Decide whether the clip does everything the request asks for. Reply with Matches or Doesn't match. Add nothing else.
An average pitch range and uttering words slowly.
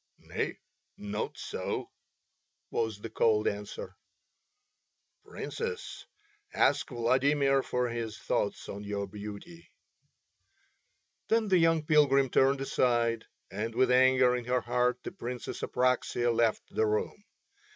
Matches